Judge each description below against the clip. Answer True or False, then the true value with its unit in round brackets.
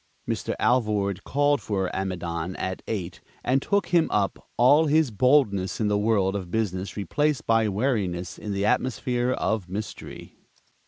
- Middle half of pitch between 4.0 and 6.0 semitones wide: True (5.0 semitones)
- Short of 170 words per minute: True (150 wpm)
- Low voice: True (105 Hz)